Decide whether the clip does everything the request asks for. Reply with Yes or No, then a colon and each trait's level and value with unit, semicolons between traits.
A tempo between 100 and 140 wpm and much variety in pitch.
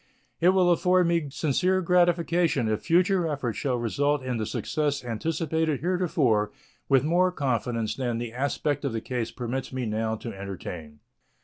No: average, 155 wpm; wide, 6.4 semitones